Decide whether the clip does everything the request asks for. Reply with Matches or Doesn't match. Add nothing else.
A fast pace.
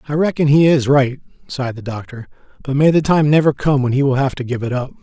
Matches